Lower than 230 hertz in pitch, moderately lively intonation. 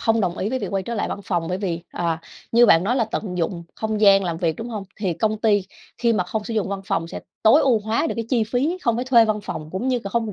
Yes: high, 215 Hz; average, 3.9 semitones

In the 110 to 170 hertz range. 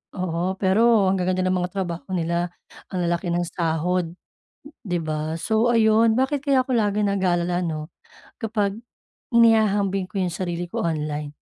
No: medium, 185 Hz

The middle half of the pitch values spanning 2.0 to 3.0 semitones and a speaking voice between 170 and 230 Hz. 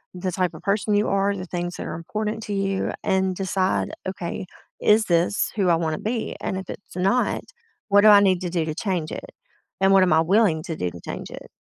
Yes: narrow, 2.6 semitones; high, 190 Hz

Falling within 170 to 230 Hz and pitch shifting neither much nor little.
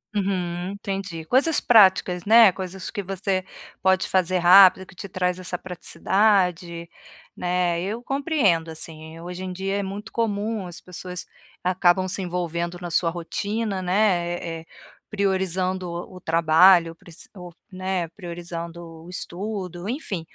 No: medium, 185 Hz; narrow, 2.1 semitones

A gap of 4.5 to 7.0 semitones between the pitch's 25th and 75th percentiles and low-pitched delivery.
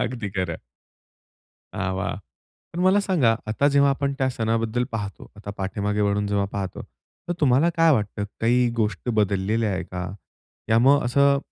Yes: average, 5.3 semitones; low, 115 Hz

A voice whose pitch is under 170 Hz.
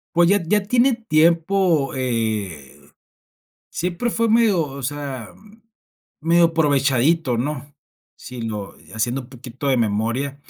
Yes: medium, 140 Hz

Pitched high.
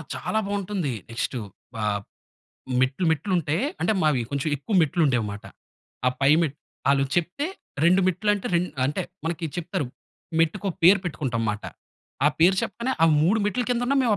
No: medium, 165 Hz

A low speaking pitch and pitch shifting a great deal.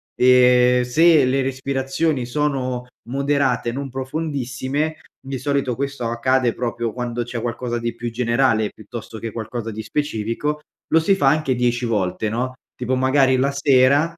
No: low, 130 Hz; average, 2.7 semitones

